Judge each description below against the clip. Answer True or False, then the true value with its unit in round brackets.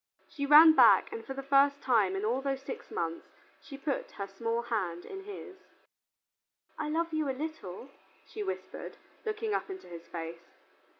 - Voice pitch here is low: False (275 Hz)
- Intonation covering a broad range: True (7.9 semitones)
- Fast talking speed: False (175 wpm)